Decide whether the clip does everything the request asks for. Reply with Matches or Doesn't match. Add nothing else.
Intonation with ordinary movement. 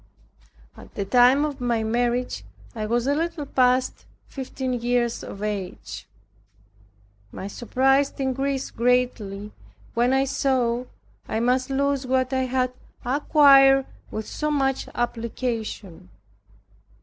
Doesn't match